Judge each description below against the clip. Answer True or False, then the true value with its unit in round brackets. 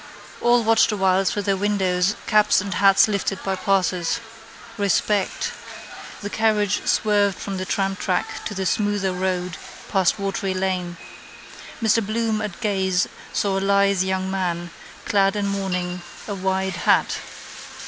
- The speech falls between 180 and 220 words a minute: False (140 wpm)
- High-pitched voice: True (195 Hz)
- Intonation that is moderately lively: False (1.7 semitones)